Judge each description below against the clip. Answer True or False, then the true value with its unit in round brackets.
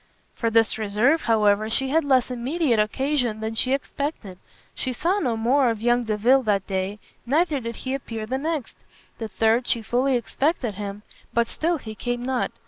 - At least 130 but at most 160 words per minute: False (180 wpm)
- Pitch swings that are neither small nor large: True (3.8 semitones)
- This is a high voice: True (240 Hz)